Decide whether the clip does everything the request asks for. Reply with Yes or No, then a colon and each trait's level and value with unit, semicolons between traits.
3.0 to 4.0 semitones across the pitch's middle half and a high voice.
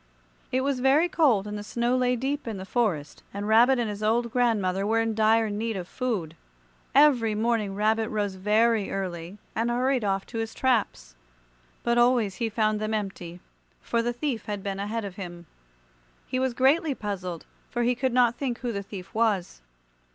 Yes: average, 3.3 semitones; high, 225 Hz